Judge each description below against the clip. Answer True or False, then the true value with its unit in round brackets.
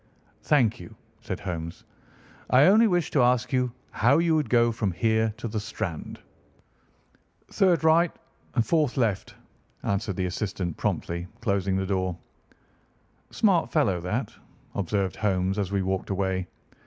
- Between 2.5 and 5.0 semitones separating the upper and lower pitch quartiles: False (5.6 semitones)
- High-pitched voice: False (105 Hz)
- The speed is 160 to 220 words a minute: False (140 wpm)